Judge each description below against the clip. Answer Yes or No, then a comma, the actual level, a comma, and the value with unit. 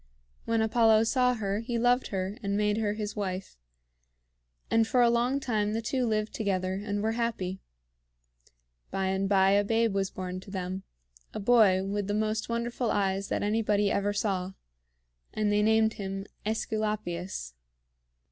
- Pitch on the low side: No, high, 210 Hz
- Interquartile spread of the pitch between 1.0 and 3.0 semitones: Yes, narrow, 2.5 semitones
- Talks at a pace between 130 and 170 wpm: Yes, average, 160 wpm